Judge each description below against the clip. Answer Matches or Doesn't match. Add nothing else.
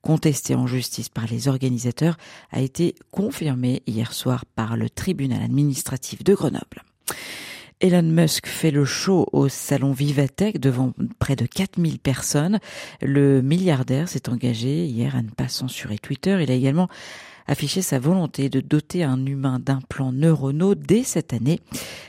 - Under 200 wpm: Matches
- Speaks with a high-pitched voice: Doesn't match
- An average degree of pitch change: Matches